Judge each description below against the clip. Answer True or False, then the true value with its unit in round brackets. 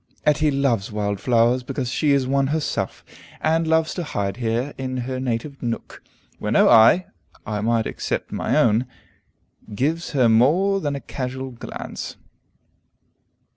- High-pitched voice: False (130 Hz)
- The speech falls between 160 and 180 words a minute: False (145 wpm)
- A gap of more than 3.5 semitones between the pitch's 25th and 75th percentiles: True (4.1 semitones)